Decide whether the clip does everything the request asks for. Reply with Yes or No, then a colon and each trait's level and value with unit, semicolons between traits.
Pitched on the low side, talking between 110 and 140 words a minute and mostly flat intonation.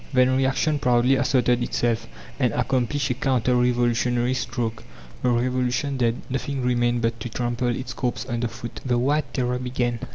No: low, 125 Hz; average, 160 wpm; narrow, 1.3 semitones